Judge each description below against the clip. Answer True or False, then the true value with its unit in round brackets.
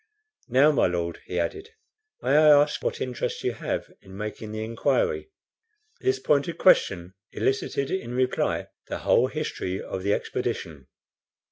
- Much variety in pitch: True (7.4 semitones)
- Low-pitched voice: True (125 Hz)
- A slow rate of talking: False (145 wpm)